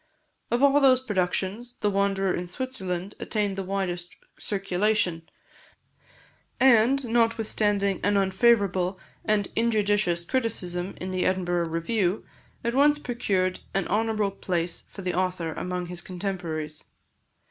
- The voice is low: No, high, 195 Hz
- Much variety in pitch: No, average, 3.7 semitones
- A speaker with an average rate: No, slow, 120 wpm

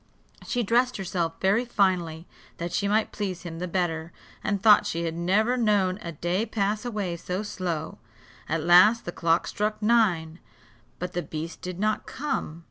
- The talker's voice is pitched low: No, medium, 185 Hz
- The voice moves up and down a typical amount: Yes, average, 3.9 semitones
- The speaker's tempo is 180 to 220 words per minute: No, average, 170 wpm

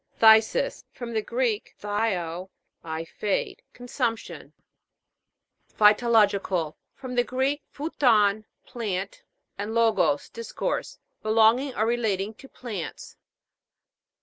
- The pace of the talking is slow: Yes, slow, 95 wpm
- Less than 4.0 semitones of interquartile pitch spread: Yes, average, 3.3 semitones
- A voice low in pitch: No, high, 220 Hz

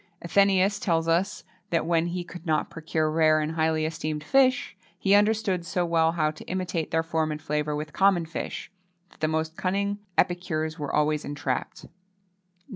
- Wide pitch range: No, average, 2.8 semitones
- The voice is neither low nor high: Yes, medium, 165 Hz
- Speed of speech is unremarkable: Yes, average, 170 wpm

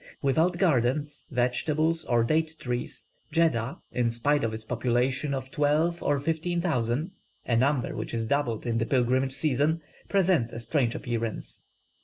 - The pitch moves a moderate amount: Yes, average, 4.7 semitones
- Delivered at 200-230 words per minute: No, average, 150 wpm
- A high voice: No, low, 135 Hz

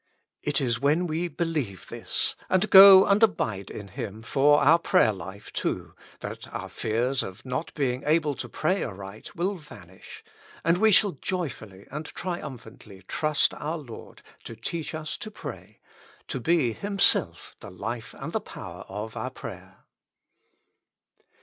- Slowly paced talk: No, average, 150 wpm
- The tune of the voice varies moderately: No, wide, 7.5 semitones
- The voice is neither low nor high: Yes, medium, 145 Hz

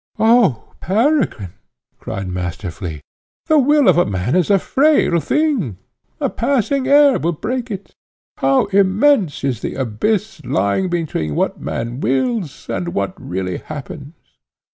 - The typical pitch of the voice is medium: Yes, medium, 175 Hz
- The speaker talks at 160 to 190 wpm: No, slow, 135 wpm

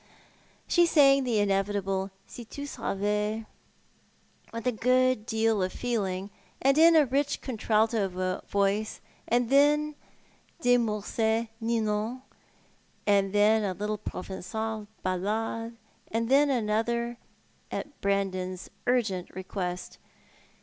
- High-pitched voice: Yes, high, 220 Hz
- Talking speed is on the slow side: Yes, slow, 115 wpm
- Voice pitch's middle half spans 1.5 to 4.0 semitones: Yes, average, 3.6 semitones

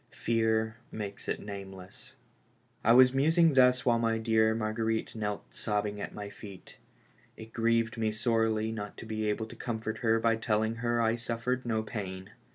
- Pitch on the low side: Yes, low, 110 Hz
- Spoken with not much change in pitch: Yes, narrow, 1.3 semitones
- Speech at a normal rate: Yes, average, 170 wpm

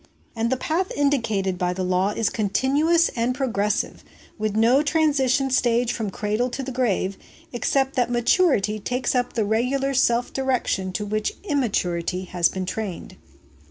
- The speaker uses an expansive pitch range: No, average, 4.6 semitones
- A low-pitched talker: No, high, 235 Hz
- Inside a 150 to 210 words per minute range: Yes, average, 160 wpm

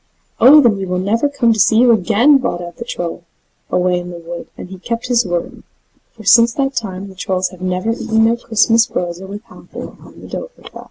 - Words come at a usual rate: No, fast, 215 wpm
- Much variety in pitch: No, average, 4.4 semitones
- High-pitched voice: Yes, high, 215 Hz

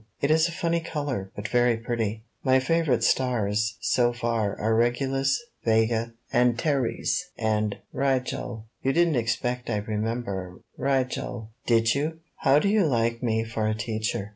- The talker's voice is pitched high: No, low, 120 Hz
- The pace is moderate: Yes, average, 145 wpm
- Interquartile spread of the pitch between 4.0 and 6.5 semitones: No, average, 3.4 semitones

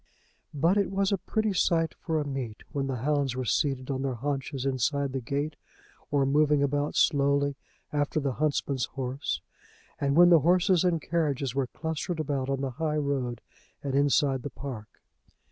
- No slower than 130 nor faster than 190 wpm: Yes, average, 175 wpm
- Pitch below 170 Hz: Yes, medium, 140 Hz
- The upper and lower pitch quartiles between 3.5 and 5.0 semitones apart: No, narrow, 2.4 semitones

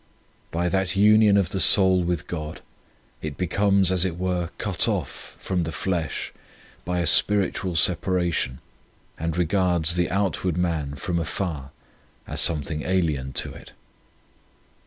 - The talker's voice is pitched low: Yes, very low, 90 Hz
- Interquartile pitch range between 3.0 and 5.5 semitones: No, narrow, 2.5 semitones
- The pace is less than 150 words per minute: Yes, average, 140 wpm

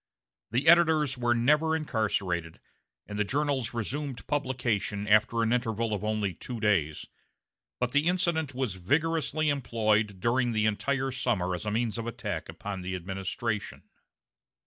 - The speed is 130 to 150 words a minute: Yes, average, 145 wpm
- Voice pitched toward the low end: Yes, low, 115 Hz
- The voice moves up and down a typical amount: Yes, average, 5.0 semitones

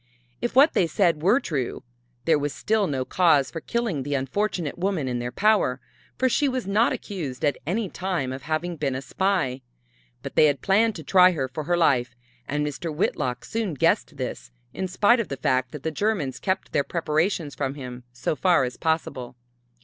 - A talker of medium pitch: Yes, medium, 160 Hz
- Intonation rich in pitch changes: Yes, wide, 6.3 semitones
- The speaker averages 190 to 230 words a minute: Yes, average, 195 wpm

